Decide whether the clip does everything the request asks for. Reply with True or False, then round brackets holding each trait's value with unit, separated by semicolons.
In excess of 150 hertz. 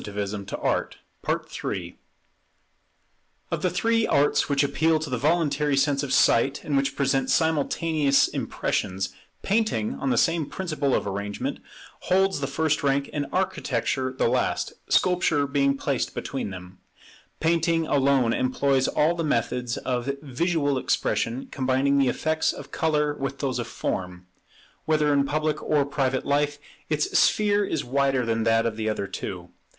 False (140 Hz)